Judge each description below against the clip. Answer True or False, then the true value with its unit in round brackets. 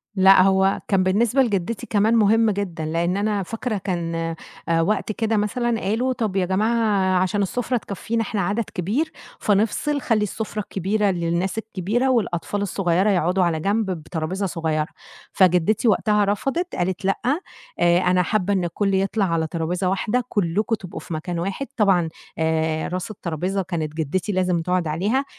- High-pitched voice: True (195 Hz)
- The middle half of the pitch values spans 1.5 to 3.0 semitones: False (3.6 semitones)